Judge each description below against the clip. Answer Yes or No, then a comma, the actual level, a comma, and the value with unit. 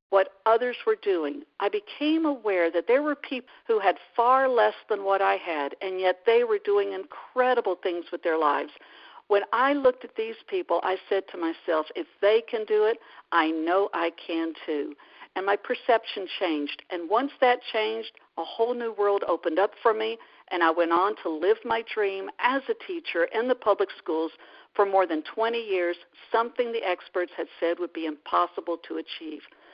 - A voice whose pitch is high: Yes, high, 205 Hz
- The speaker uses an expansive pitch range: Yes, wide, 6.6 semitones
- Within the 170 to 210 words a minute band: Yes, average, 190 wpm